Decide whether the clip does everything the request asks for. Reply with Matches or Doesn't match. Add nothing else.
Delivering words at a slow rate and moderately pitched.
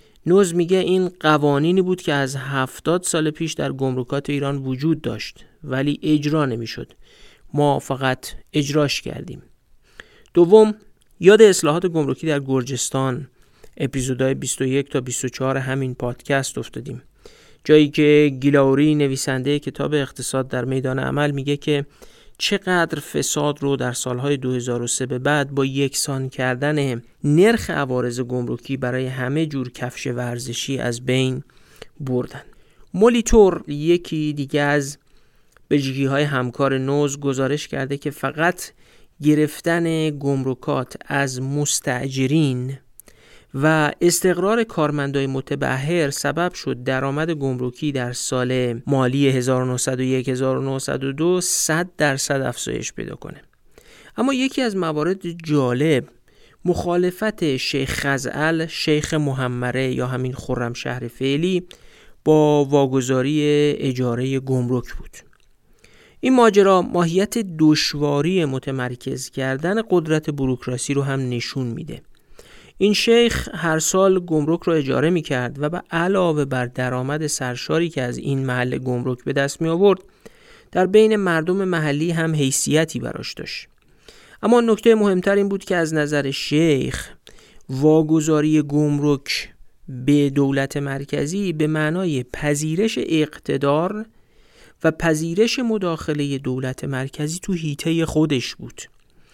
Doesn't match